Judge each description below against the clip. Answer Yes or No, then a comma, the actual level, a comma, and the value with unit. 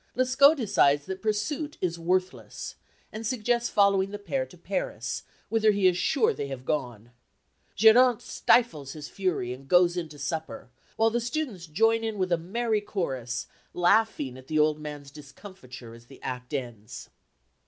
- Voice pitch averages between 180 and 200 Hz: Yes, medium, 185 Hz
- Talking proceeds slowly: No, average, 165 wpm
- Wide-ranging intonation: Yes, wide, 7.9 semitones